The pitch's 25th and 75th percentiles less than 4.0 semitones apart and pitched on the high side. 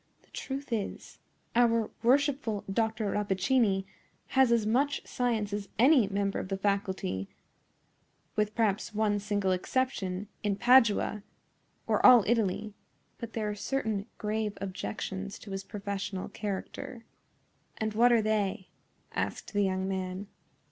Yes: average, 2.8 semitones; high, 210 Hz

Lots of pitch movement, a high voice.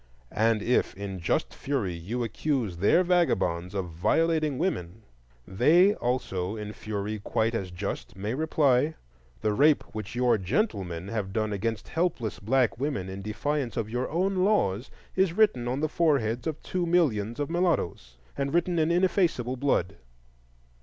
No: wide, 7.8 semitones; low, 120 Hz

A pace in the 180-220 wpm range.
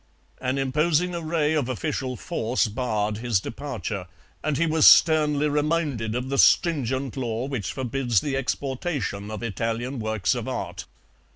No: average, 145 wpm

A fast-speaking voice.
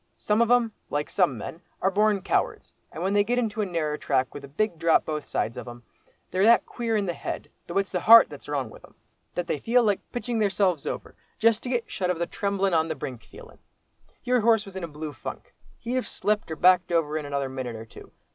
Yes: fast, 240 wpm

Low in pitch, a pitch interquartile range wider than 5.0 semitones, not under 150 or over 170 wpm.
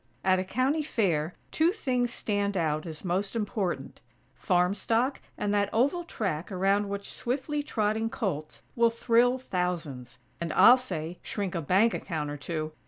No: high, 200 Hz; wide, 5.4 semitones; average, 160 wpm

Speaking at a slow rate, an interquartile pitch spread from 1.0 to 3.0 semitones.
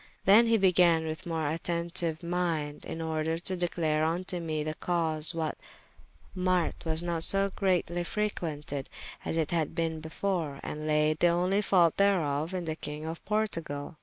No: average, 165 wpm; narrow, 2.4 semitones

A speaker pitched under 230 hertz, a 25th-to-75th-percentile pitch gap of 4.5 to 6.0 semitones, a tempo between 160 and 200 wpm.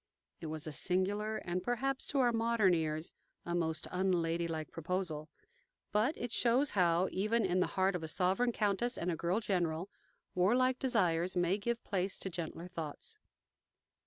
Yes: medium, 185 Hz; average, 4.9 semitones; average, 165 wpm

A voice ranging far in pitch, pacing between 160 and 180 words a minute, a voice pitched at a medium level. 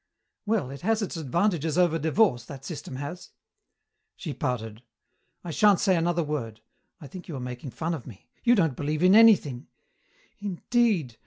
Yes: wide, 5.8 semitones; average, 170 wpm; medium, 160 Hz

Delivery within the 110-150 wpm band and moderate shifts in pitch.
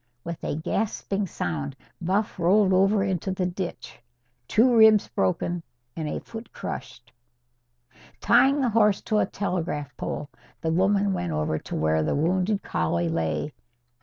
No: average, 145 wpm; wide, 6.5 semitones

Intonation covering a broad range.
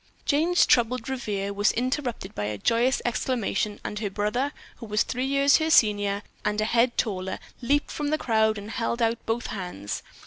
No: average, 3.8 semitones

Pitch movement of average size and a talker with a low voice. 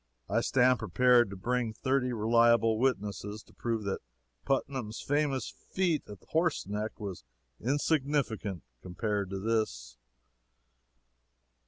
Yes: average, 4.2 semitones; low, 115 Hz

